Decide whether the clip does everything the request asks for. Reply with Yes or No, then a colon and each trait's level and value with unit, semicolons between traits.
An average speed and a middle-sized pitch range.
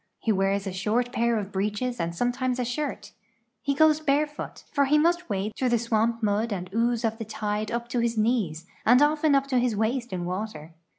No: fast, 220 wpm; average, 3.6 semitones